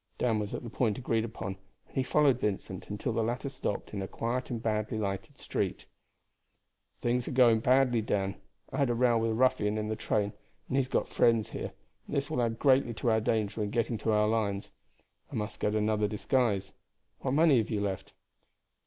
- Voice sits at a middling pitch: No, low, 115 Hz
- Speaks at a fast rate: Yes, fast, 210 wpm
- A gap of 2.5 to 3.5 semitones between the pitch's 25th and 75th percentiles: Yes, average, 3.0 semitones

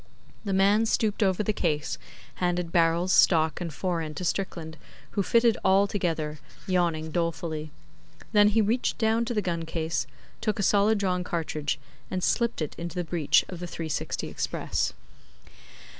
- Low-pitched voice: No, medium, 180 Hz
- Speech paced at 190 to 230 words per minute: No, average, 160 wpm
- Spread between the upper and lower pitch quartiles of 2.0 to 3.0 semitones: No, average, 3.8 semitones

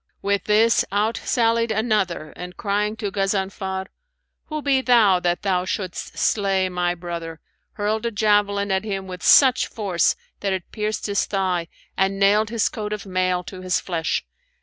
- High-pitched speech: Yes, high, 200 Hz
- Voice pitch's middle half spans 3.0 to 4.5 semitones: No, narrow, 2.6 semitones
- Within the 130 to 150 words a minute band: No, average, 165 wpm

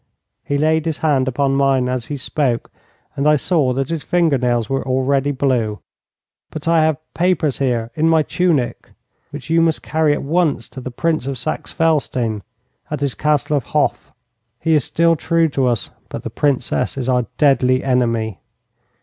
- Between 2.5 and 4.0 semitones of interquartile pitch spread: Yes, average, 3.7 semitones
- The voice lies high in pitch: No, medium, 140 Hz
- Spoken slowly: No, average, 180 wpm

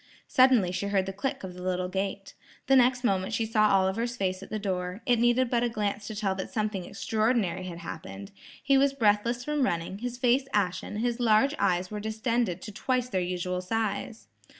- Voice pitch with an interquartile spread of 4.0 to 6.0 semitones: Yes, average, 4.3 semitones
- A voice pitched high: Yes, high, 210 Hz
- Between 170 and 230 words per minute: Yes, average, 200 wpm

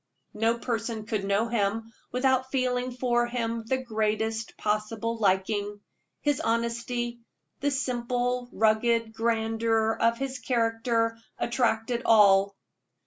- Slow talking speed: Yes, slow, 110 wpm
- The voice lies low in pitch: No, high, 230 Hz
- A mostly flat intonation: Yes, narrow, 1.7 semitones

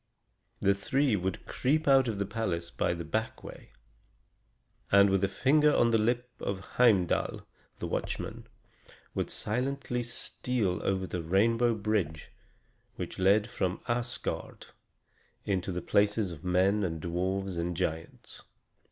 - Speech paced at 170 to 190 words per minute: No, slow, 135 wpm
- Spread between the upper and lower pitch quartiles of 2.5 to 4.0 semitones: No, average, 4.6 semitones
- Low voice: Yes, low, 100 Hz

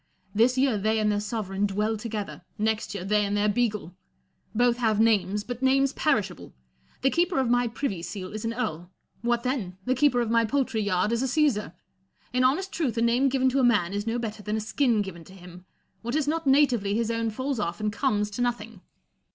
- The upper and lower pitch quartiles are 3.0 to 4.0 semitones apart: Yes, average, 3.5 semitones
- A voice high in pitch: Yes, high, 225 Hz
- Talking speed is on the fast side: Yes, fast, 220 wpm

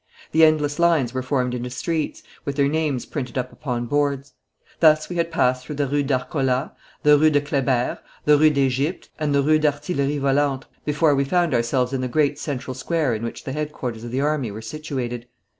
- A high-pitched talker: No, medium, 140 Hz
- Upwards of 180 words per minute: Yes, average, 200 wpm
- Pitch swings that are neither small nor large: Yes, average, 3.0 semitones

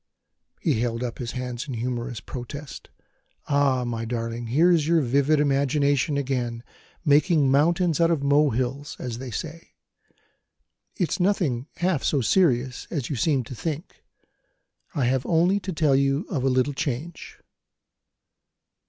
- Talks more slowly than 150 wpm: Yes, average, 140 wpm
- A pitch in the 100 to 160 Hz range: Yes, medium, 140 Hz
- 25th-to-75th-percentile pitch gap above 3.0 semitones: Yes, average, 3.9 semitones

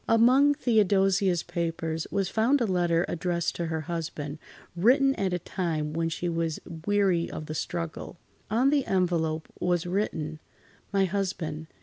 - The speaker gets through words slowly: No, average, 145 wpm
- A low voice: No, medium, 175 Hz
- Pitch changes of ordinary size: Yes, average, 3.7 semitones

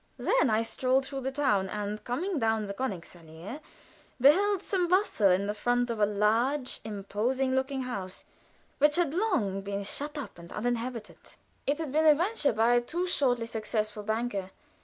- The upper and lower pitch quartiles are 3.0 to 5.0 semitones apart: No, wide, 5.5 semitones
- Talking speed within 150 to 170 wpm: Yes, average, 165 wpm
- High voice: Yes, high, 245 Hz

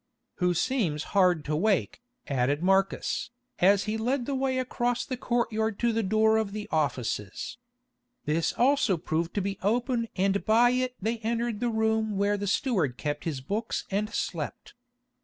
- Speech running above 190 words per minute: No, average, 165 wpm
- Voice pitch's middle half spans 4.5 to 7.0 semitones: Yes, average, 4.8 semitones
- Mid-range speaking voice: No, high, 215 Hz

